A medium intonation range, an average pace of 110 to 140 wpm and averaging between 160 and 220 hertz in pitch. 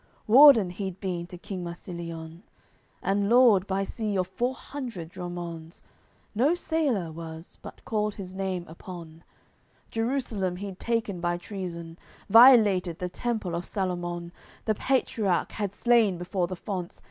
Yes: average, 4.0 semitones; slow, 135 wpm; high, 190 Hz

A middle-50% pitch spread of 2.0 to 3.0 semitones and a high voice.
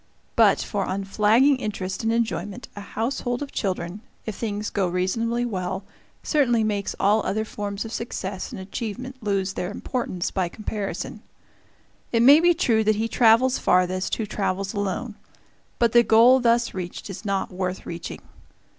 No: average, 3.5 semitones; high, 215 Hz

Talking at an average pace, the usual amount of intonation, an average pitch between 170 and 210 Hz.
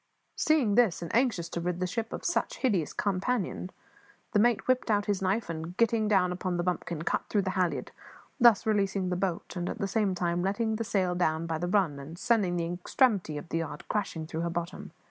No: fast, 220 wpm; average, 3.7 semitones; medium, 185 Hz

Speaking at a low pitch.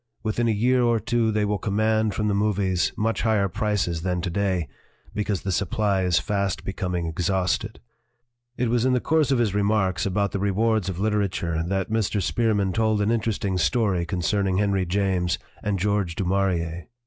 Yes: low, 100 Hz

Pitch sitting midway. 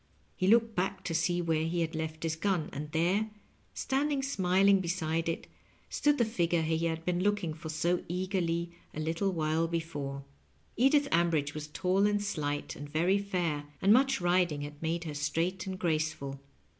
Yes: medium, 170 Hz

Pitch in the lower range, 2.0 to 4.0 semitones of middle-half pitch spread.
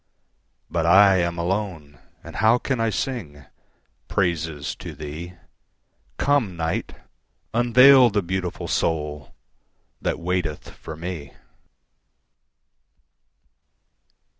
No: very low, 85 Hz; average, 5.0 semitones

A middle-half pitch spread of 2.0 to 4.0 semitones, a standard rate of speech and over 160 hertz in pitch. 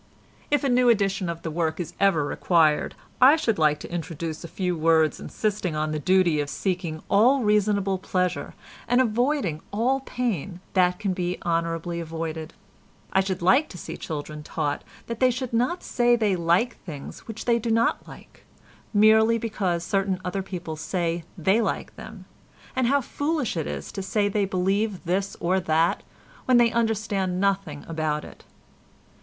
No: average, 5.1 semitones; average, 170 wpm; high, 190 Hz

